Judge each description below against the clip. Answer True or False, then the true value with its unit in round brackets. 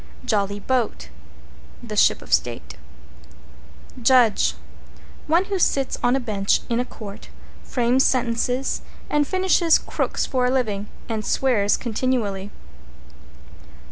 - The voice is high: True (240 Hz)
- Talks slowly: True (115 wpm)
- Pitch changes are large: False (4.3 semitones)